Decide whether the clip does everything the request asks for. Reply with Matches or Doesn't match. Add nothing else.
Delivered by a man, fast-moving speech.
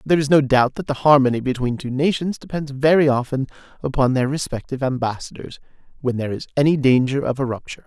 Doesn't match